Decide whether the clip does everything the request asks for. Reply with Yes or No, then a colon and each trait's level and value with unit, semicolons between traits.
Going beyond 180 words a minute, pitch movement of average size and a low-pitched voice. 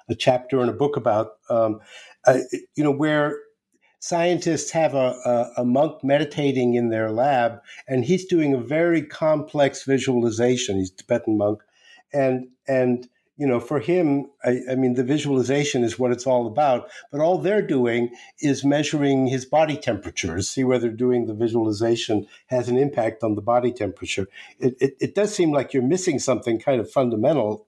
No: average, 175 wpm; average, 3.6 semitones; low, 130 Hz